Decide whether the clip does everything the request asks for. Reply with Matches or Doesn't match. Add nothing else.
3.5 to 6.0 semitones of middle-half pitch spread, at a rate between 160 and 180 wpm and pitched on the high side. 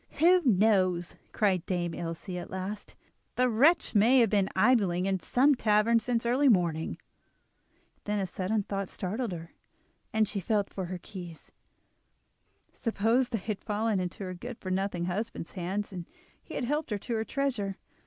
Matches